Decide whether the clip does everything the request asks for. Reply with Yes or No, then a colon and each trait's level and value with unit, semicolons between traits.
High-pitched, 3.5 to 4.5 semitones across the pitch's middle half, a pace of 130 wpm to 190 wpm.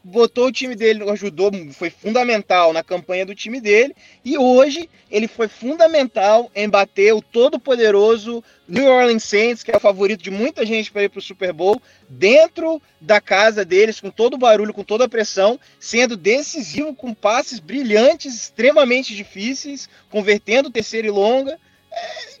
Yes: high, 225 Hz; average, 4.2 semitones; average, 165 wpm